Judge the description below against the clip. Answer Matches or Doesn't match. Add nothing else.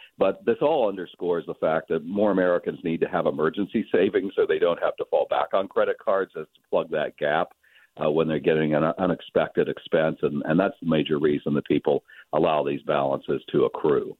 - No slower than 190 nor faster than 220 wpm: Matches